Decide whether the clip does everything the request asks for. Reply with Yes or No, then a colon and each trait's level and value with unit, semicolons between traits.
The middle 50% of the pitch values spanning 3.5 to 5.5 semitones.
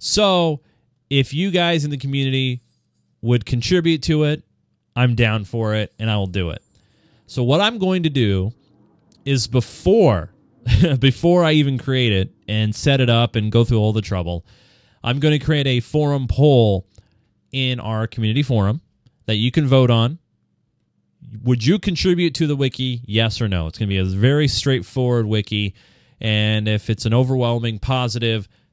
Yes: average, 4.4 semitones